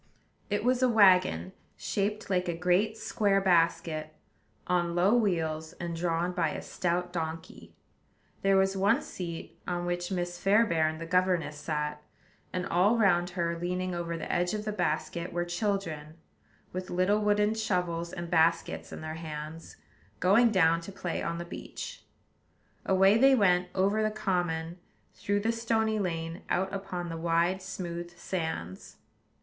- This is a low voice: No, medium, 180 Hz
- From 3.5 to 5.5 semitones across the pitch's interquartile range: No, average, 2.9 semitones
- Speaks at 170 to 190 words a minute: No, average, 155 wpm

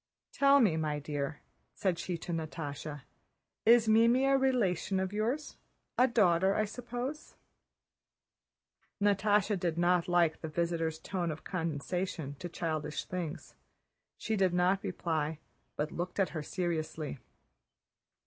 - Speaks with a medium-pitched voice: Yes, medium, 180 Hz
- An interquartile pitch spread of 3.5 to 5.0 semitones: Yes, average, 4.5 semitones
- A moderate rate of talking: No, slow, 130 wpm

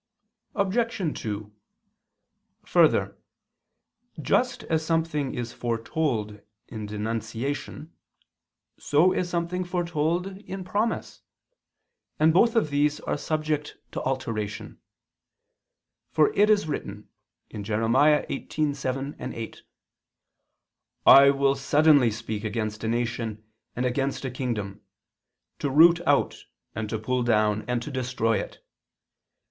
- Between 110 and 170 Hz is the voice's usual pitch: Yes, low, 135 Hz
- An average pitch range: No, wide, 5.9 semitones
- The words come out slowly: Yes, slow, 110 wpm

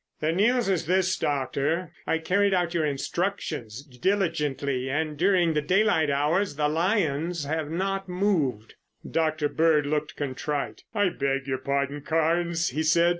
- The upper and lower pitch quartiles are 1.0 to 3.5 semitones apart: No, average, 4.0 semitones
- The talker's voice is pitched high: No, medium, 160 Hz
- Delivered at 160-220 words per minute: No, average, 145 wpm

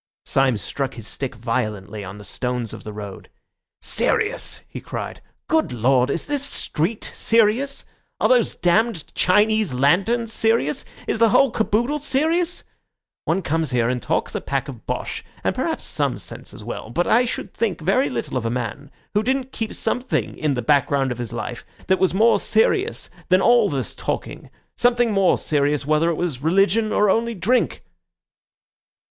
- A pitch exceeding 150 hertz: Yes, medium, 185 Hz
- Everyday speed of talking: Yes, average, 170 wpm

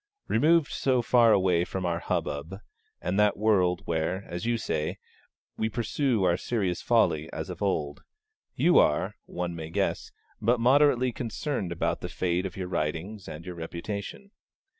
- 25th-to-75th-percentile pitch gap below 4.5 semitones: No, wide, 5.4 semitones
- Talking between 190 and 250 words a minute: No, average, 160 wpm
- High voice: No, very low, 95 Hz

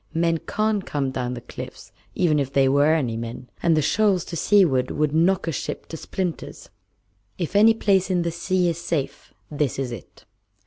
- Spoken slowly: No, average, 190 wpm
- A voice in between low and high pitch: Yes, medium, 160 Hz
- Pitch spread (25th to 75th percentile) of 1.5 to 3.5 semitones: No, average, 5.1 semitones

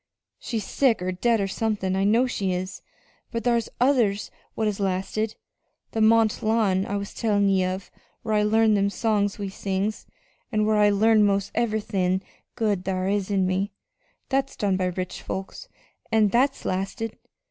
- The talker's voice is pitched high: Yes, high, 205 Hz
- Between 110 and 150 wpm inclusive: No, average, 170 wpm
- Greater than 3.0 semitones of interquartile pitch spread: No, narrow, 2.5 semitones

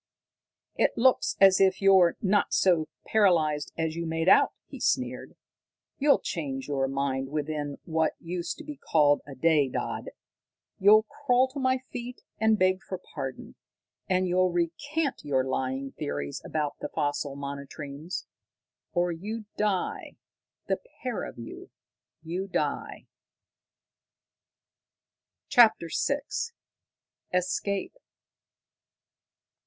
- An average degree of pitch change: No, wide, 5.8 semitones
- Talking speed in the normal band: No, slow, 115 wpm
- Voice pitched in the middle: Yes, medium, 170 Hz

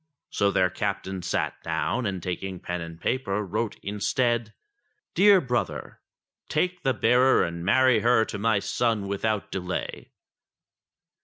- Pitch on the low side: Yes, low, 105 Hz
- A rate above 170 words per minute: No, slow, 135 wpm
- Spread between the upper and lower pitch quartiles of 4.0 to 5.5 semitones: Yes, average, 4.3 semitones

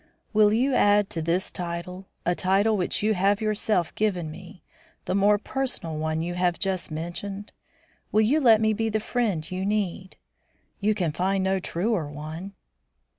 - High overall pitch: Yes, high, 195 Hz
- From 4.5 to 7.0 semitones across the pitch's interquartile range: No, average, 3.5 semitones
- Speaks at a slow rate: No, average, 170 wpm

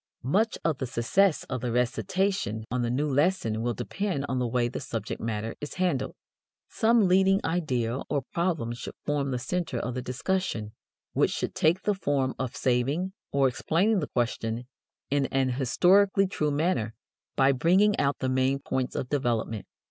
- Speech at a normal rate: Yes, average, 170 wpm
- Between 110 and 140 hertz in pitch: Yes, low, 135 Hz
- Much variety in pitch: Yes, wide, 6.6 semitones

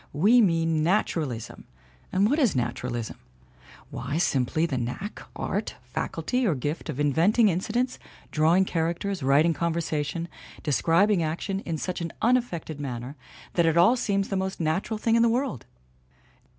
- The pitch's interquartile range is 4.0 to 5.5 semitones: Yes, average, 5.1 semitones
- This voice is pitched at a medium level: Yes, medium, 170 Hz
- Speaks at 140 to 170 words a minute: Yes, average, 150 wpm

